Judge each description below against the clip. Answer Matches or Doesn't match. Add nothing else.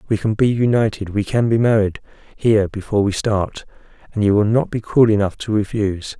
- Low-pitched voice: Matches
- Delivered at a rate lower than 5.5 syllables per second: Doesn't match